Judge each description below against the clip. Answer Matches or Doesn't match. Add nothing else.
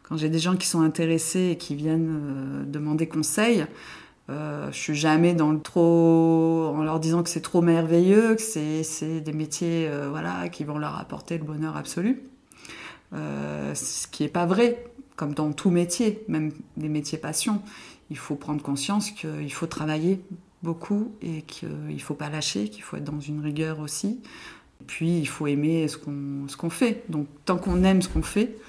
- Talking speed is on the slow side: Doesn't match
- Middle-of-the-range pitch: Matches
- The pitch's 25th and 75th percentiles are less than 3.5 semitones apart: Matches